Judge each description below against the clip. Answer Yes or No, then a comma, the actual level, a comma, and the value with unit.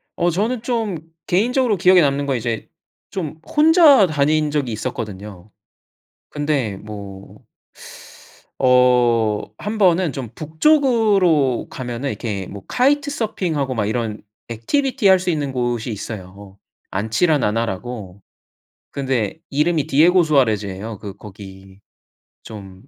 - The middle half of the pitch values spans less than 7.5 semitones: No, wide, 8.7 semitones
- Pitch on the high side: No, low, 130 Hz